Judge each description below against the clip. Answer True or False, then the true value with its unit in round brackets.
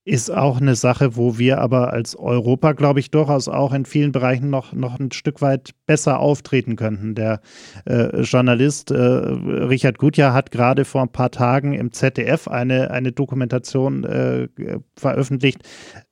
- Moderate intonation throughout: False (2.1 semitones)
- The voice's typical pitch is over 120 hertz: True (130 Hz)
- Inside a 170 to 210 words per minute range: False (160 wpm)